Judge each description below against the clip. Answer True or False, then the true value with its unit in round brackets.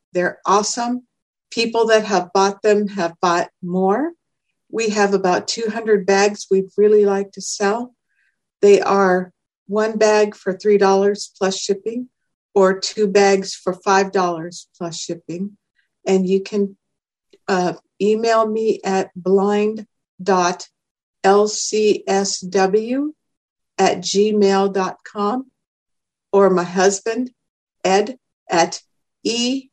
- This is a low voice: False (200 Hz)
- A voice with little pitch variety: True (2.3 semitones)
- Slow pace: True (105 wpm)